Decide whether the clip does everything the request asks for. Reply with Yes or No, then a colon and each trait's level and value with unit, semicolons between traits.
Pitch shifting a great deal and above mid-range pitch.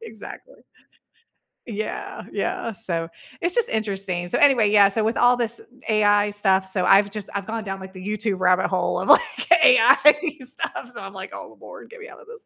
No: average, 4.3 semitones; high, 210 Hz